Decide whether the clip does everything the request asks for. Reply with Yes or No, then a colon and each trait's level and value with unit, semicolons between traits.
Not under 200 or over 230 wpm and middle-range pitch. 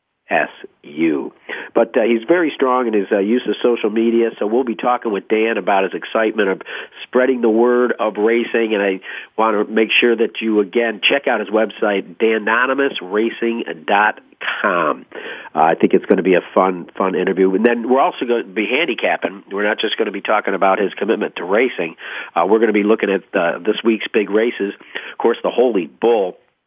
No: fast, 205 wpm; low, 115 Hz